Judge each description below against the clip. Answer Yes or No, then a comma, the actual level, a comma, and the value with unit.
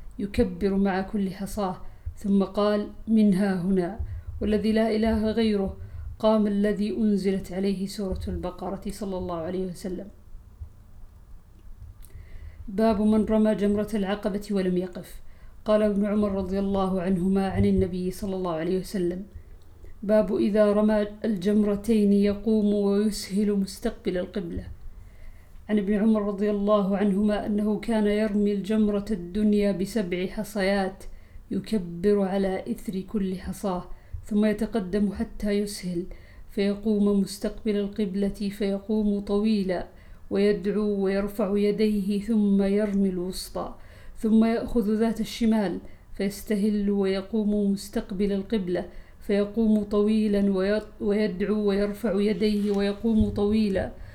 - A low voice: No, high, 205 Hz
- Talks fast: No, average, 105 wpm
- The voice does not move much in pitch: Yes, narrow, 2.0 semitones